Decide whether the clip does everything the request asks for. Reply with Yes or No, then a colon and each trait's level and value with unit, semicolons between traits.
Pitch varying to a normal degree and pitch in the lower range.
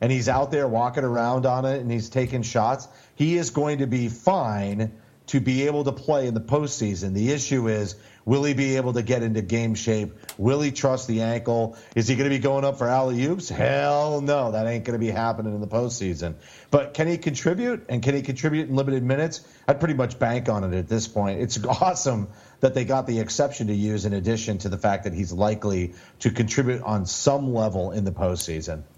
Yes: average, 4.2 semitones; low, 120 Hz